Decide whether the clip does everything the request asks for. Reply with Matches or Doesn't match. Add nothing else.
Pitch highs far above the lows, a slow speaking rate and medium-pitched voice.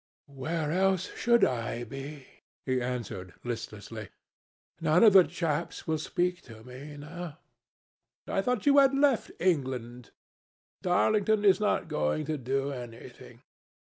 Matches